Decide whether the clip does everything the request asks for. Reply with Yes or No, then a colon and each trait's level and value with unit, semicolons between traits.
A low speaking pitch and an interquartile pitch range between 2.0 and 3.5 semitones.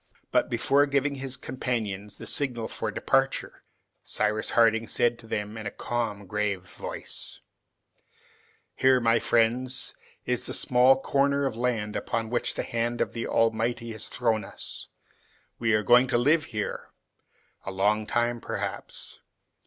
Yes: low, 115 Hz; average, 2.8 semitones